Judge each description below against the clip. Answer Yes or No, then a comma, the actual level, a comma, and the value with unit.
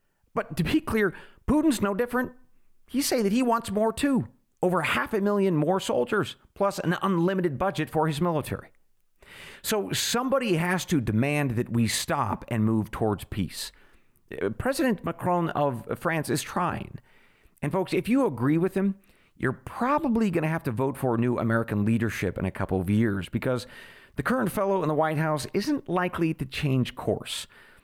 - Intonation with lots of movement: Yes, wide, 8.8 semitones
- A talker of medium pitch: Yes, medium, 165 Hz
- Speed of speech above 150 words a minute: Yes, average, 175 wpm